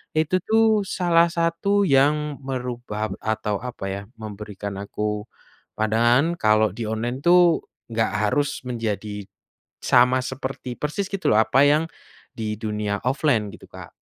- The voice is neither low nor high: No, low, 125 Hz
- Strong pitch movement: Yes, wide, 6.1 semitones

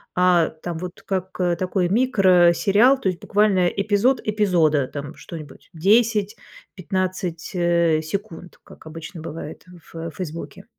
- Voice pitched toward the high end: No, medium, 180 Hz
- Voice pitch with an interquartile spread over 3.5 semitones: No, average, 3.1 semitones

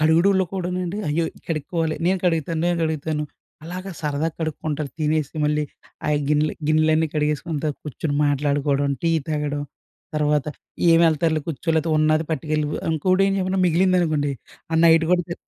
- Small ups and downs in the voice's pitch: Yes, narrow, 2.1 semitones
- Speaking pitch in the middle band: Yes, medium, 155 Hz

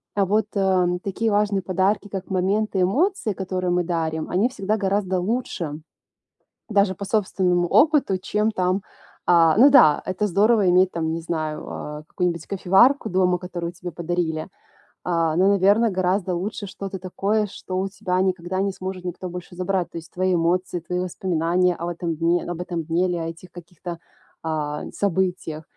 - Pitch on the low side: No, medium, 185 Hz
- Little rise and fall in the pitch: Yes, narrow, 2.3 semitones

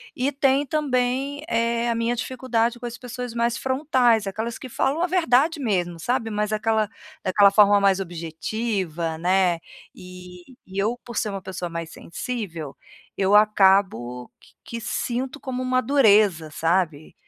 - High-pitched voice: Yes, high, 220 Hz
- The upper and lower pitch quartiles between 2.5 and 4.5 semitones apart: No, average, 5.1 semitones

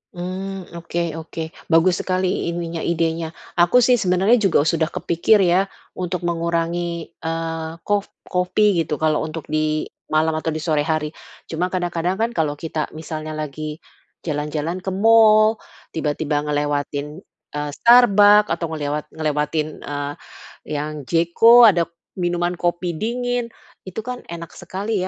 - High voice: No, medium, 170 Hz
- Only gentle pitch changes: No, average, 3.1 semitones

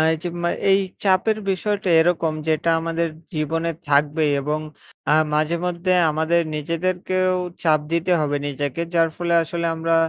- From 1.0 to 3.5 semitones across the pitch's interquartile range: Yes, narrow, 2.4 semitones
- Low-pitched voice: No, medium, 165 Hz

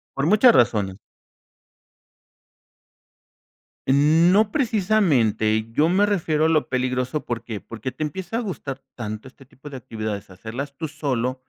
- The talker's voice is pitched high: No, low, 135 Hz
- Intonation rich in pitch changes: Yes, wide, 6.4 semitones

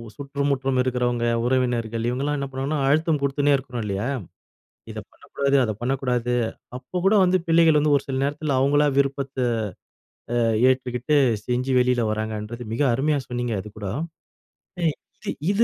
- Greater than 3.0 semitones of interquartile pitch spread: No, narrow, 2.6 semitones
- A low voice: Yes, low, 130 Hz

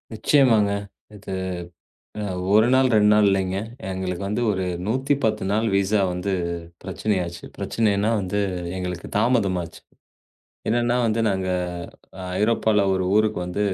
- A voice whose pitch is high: No, low, 105 Hz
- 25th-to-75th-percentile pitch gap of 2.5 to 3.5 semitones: Yes, average, 2.8 semitones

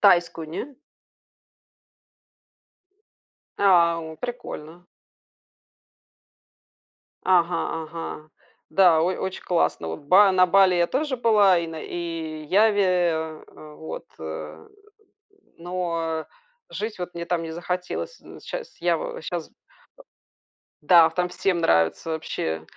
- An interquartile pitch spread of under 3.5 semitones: Yes, average, 2.9 semitones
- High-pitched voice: No, medium, 170 Hz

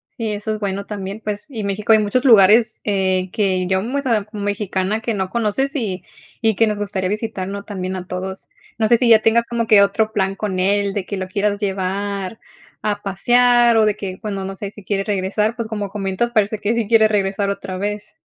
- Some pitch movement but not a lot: No, narrow, 2.3 semitones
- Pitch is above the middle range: Yes, high, 205 Hz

